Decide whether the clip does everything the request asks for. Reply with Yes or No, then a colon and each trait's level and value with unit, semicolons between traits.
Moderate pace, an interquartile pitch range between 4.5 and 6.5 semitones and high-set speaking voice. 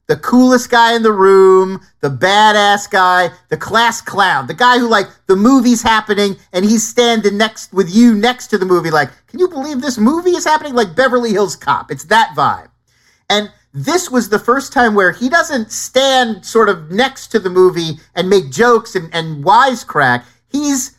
Yes: average, 190 wpm; average, 4.8 semitones; high, 220 Hz